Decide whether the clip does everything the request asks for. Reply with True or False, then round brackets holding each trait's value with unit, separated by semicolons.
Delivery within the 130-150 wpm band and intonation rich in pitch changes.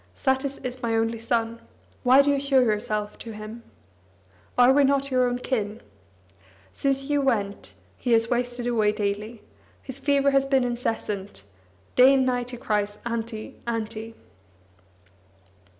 False (145 wpm; 3.2 semitones)